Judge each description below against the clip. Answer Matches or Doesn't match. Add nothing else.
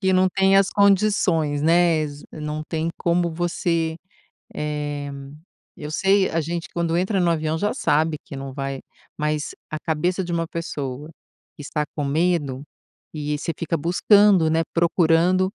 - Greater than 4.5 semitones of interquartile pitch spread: Doesn't match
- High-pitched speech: Doesn't match